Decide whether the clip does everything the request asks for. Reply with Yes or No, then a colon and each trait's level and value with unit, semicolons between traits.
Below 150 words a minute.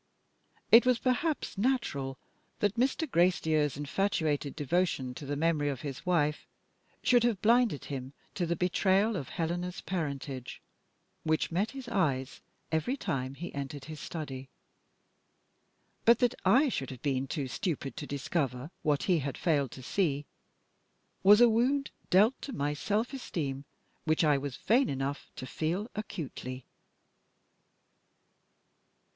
Yes: average, 140 wpm